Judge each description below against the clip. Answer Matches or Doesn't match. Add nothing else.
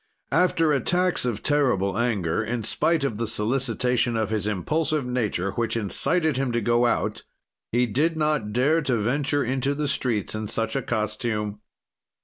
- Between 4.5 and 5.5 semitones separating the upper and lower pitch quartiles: Matches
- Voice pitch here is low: Matches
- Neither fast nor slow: Matches